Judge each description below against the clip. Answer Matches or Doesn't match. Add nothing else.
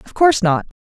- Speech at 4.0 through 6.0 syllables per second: Doesn't match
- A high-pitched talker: Matches